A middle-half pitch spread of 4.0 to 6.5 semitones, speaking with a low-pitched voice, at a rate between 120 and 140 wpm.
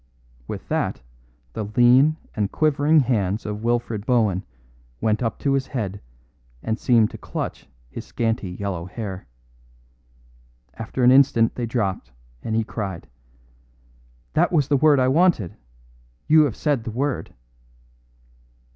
Yes: average, 4.4 semitones; low, 115 Hz; slow, 135 wpm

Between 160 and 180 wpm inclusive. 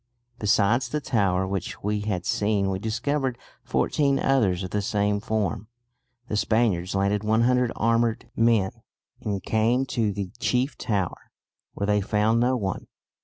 No: average, 145 wpm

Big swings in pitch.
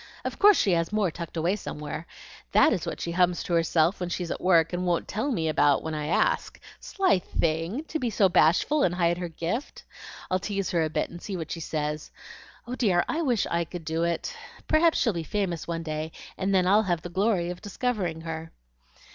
No: average, 3.7 semitones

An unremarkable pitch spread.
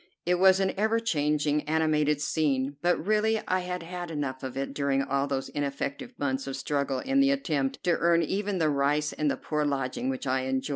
Yes: average, 4.5 semitones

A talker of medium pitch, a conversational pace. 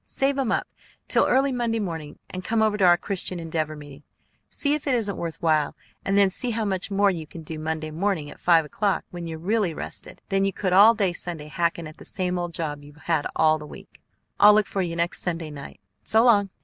No: medium, 180 Hz; fast, 235 wpm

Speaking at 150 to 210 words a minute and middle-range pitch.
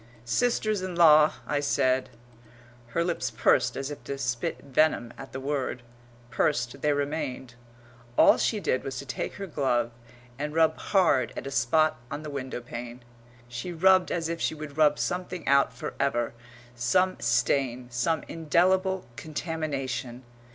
Yes: average, 155 wpm; medium, 145 Hz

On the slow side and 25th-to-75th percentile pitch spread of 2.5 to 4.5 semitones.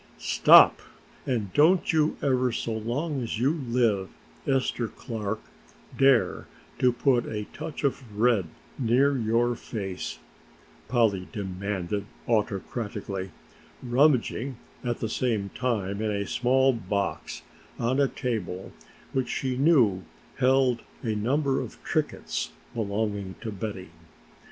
Yes: slow, 115 wpm; average, 4.1 semitones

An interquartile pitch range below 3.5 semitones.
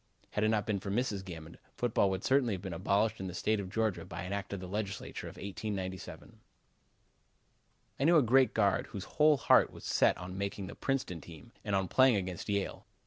Yes: average, 3.0 semitones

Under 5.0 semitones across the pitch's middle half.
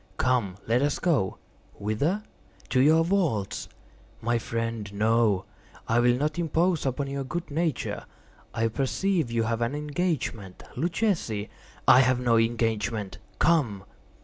No: wide, 5.5 semitones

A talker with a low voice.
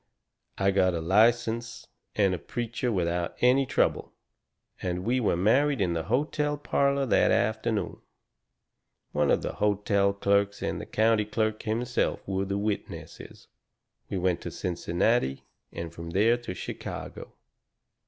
Yes: low, 105 Hz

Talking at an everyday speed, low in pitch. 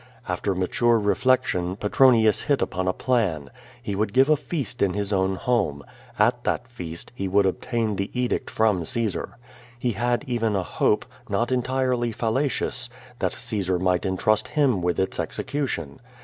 Yes: average, 160 wpm; low, 110 Hz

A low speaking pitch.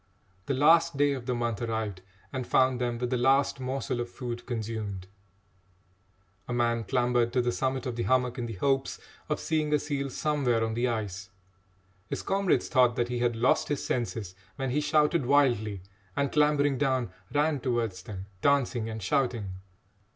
Yes: low, 125 Hz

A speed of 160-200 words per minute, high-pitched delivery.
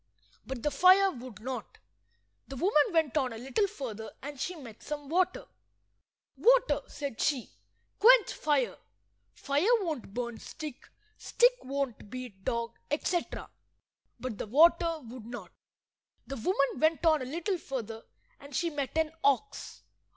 No: average, 145 wpm; very high, 280 Hz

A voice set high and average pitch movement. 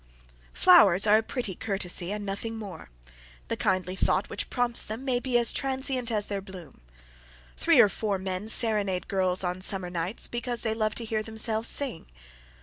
Yes: high, 210 Hz; average, 3.5 semitones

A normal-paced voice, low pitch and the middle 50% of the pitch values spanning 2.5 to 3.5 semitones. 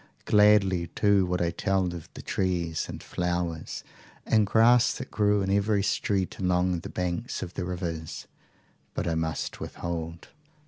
Yes: average, 150 wpm; very low, 90 Hz; average, 2.9 semitones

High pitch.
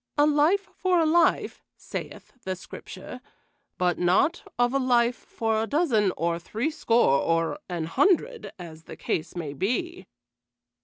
Yes: high, 225 Hz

